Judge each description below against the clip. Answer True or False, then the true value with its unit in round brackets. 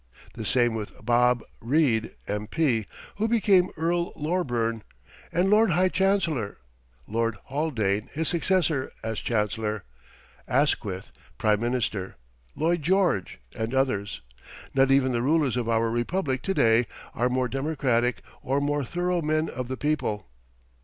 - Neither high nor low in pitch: False (130 Hz)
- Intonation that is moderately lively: False (6.1 semitones)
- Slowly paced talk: True (130 wpm)